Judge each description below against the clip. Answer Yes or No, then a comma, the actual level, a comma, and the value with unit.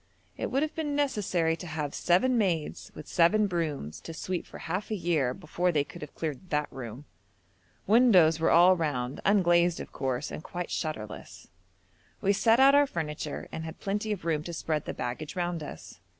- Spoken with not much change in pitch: No, average, 4.5 semitones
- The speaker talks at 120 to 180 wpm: No, average, 190 wpm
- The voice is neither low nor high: Yes, medium, 170 Hz